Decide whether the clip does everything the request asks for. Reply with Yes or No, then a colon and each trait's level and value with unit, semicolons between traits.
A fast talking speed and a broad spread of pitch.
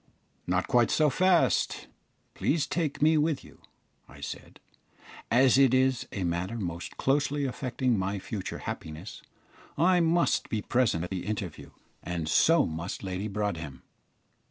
No: average, 140 wpm; wide, 7.5 semitones